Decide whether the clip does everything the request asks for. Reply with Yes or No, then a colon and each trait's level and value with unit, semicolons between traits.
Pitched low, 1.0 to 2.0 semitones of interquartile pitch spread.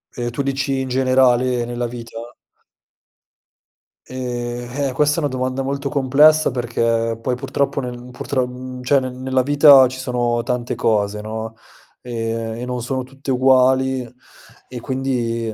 Yes: low, 125 Hz; narrow, 1.7 semitones